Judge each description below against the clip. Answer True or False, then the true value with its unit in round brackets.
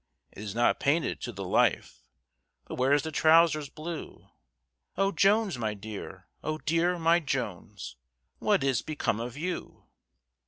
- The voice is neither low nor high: True (150 Hz)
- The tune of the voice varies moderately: False (6.2 semitones)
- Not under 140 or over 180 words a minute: True (145 wpm)